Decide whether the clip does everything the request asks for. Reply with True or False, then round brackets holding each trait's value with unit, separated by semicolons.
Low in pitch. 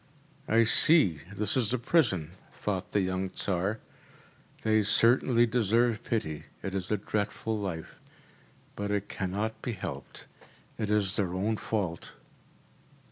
True (105 Hz)